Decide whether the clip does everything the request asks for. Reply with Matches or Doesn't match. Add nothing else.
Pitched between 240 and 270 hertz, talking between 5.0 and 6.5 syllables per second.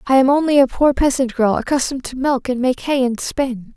Matches